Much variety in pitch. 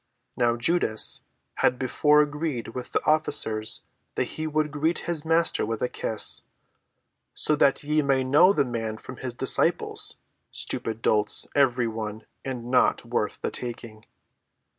No: average, 4.7 semitones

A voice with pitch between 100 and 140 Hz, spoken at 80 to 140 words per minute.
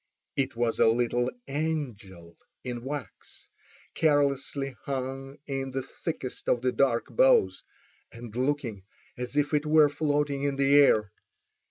Yes: low, 135 Hz; slow, 135 wpm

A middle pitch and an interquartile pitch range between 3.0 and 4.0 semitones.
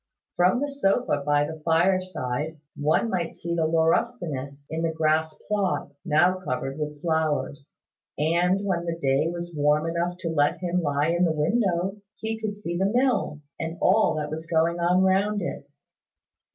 Yes: medium, 170 Hz; average, 3.4 semitones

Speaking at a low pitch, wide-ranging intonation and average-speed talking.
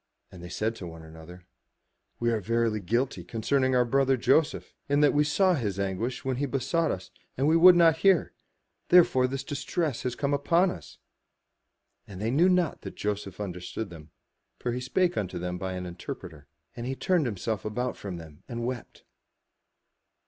Yes: low, 120 Hz; wide, 7.2 semitones; average, 180 wpm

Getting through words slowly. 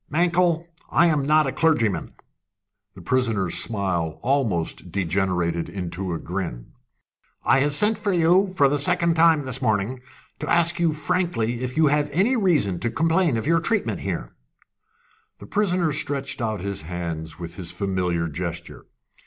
No: average, 155 wpm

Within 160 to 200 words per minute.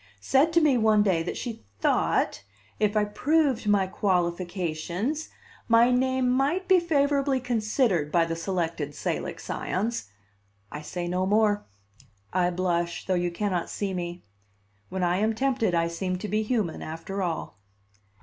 No: average, 150 wpm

